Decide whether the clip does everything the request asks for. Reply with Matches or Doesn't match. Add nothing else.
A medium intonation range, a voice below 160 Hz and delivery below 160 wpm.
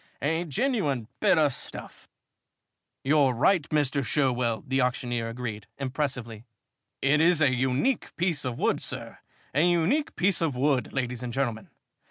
Matches